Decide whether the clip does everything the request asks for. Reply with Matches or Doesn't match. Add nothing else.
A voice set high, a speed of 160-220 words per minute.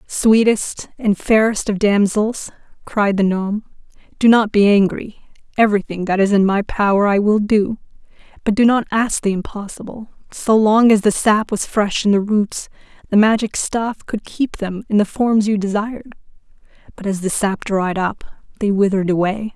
Matches